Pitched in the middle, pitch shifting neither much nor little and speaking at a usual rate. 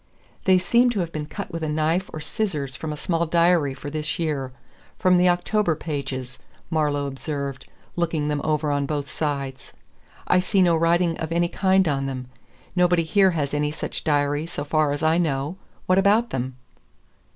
Yes: medium, 155 Hz; average, 3.4 semitones; average, 185 wpm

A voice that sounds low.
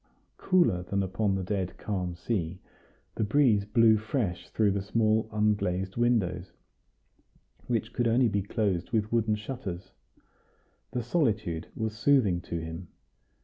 Yes: low, 105 Hz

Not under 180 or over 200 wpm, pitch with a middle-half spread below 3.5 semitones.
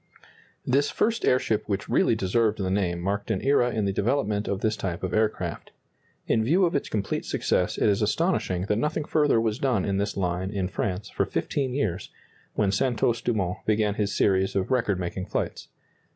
No: average, 190 wpm; average, 4.0 semitones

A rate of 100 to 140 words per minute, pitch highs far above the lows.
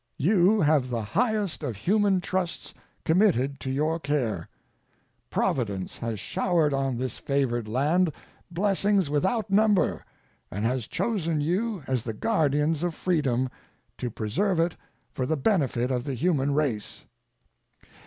Yes: slow, 135 wpm; wide, 6.4 semitones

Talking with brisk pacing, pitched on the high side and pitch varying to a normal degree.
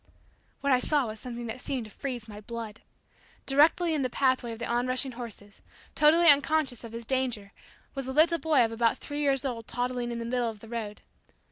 Yes: fast, 215 wpm; high, 245 Hz; average, 3.1 semitones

